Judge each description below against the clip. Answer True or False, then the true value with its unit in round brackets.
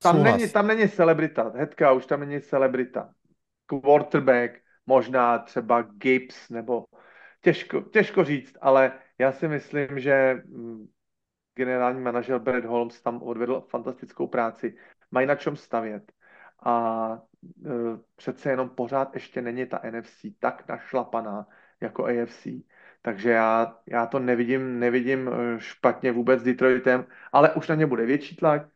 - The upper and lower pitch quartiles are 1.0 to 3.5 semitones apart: True (2.8 semitones)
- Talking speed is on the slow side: False (135 wpm)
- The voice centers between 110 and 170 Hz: True (130 Hz)